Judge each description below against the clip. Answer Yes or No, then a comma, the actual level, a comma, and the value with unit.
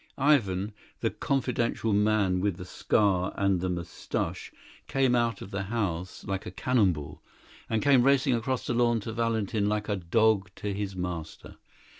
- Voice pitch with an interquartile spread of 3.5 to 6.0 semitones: Yes, average, 3.9 semitones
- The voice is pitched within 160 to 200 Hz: No, low, 105 Hz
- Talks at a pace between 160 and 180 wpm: Yes, average, 165 wpm